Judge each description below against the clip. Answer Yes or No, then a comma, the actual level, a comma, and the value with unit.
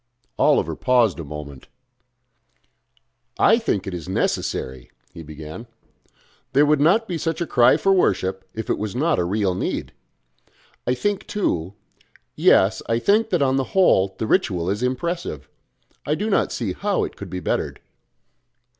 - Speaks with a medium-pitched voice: No, low, 115 Hz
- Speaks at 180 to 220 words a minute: No, average, 160 wpm